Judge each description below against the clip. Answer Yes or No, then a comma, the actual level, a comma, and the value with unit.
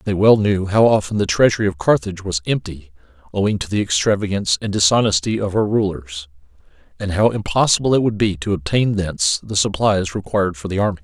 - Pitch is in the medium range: No, very low, 95 Hz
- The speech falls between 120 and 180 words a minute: No, average, 190 wpm